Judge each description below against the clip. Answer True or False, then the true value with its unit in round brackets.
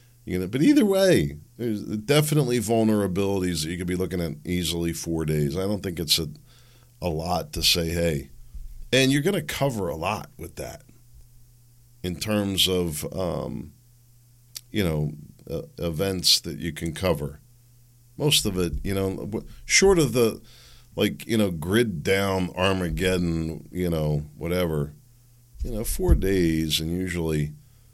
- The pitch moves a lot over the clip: True (6.5 semitones)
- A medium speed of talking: True (150 wpm)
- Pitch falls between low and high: False (95 Hz)